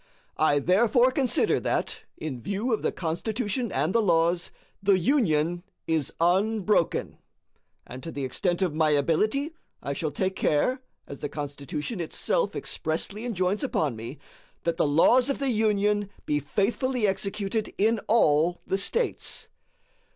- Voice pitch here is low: No, medium, 185 Hz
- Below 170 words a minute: Yes, average, 145 wpm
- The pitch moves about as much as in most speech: No, wide, 6.0 semitones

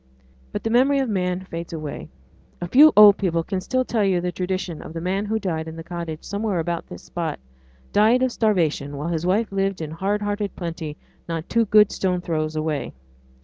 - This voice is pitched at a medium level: Yes, medium, 180 Hz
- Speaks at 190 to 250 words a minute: Yes, fast, 205 wpm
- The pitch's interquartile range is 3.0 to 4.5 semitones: Yes, average, 4.0 semitones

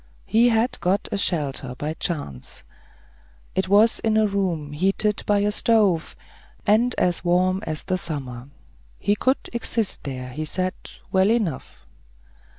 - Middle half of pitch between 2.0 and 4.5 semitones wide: No, average, 5.3 semitones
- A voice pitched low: No, high, 190 Hz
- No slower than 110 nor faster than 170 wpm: Yes, average, 140 wpm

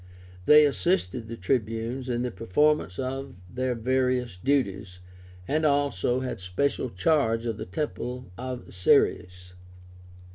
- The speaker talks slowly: Yes, slow, 120 wpm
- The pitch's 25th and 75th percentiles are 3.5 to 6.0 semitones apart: Yes, average, 5.0 semitones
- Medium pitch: No, low, 125 Hz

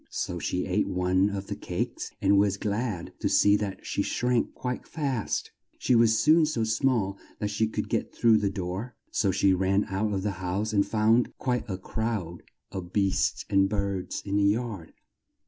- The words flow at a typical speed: Yes, average, 185 wpm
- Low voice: Yes, low, 100 Hz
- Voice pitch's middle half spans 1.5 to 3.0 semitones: Yes, average, 2.7 semitones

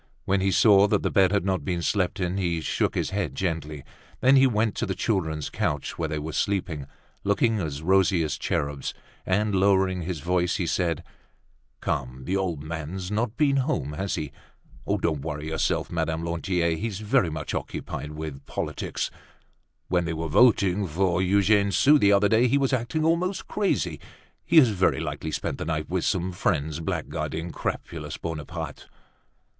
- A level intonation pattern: No, average, 4.2 semitones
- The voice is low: Yes, very low, 90 Hz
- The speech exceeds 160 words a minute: Yes, average, 175 wpm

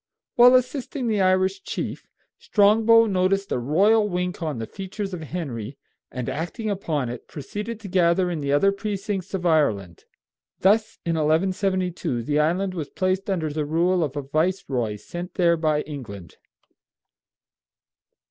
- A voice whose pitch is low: No, medium, 180 Hz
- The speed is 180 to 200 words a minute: No, average, 150 wpm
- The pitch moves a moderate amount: Yes, average, 4.8 semitones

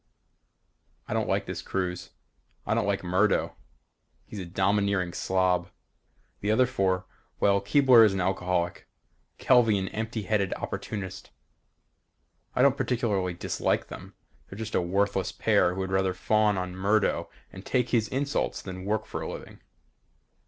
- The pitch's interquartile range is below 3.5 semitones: Yes, average, 2.8 semitones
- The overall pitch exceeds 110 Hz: No, low, 100 Hz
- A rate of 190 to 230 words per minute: No, average, 150 wpm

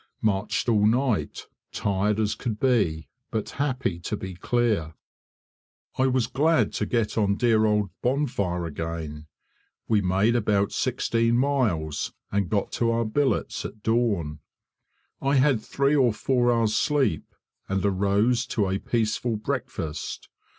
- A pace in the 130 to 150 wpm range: Yes, slow, 135 wpm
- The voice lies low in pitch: Yes, low, 110 Hz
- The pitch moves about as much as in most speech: Yes, average, 4.0 semitones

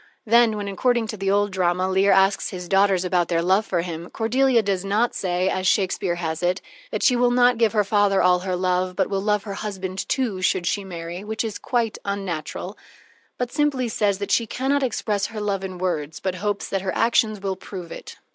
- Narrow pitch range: No, average, 3.1 semitones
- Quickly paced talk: Yes, fast, 220 wpm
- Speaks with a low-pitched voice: No, high, 195 Hz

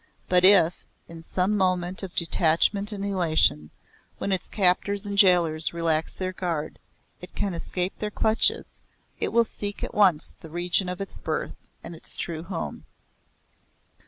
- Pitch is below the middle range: No, medium, 180 Hz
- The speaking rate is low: No, average, 155 wpm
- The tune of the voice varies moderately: Yes, average, 3.0 semitones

